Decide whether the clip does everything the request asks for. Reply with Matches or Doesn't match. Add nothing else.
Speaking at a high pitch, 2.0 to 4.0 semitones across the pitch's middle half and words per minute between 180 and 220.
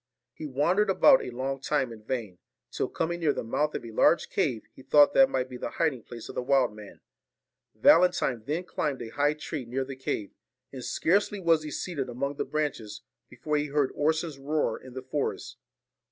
Doesn't match